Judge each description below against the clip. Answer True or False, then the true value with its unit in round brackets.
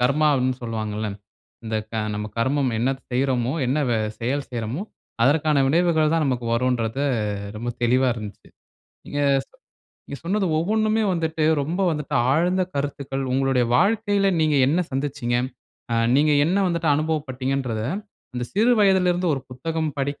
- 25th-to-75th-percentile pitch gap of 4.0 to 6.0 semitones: True (4.6 semitones)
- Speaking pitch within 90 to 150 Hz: True (140 Hz)